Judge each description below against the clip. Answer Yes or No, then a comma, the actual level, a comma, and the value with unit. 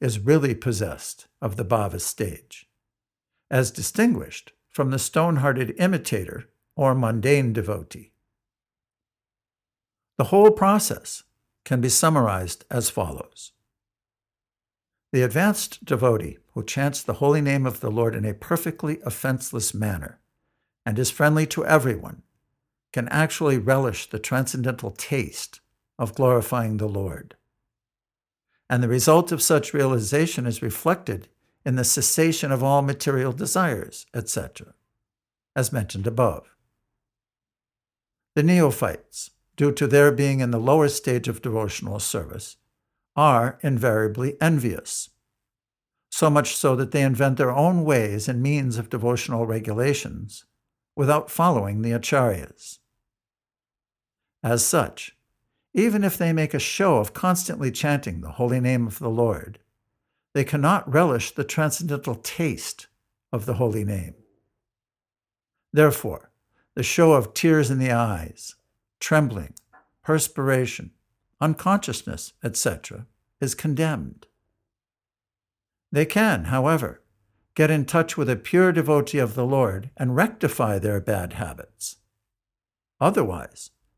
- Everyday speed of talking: No, slow, 120 wpm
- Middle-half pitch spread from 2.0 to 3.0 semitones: No, average, 5.1 semitones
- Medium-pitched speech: No, low, 125 Hz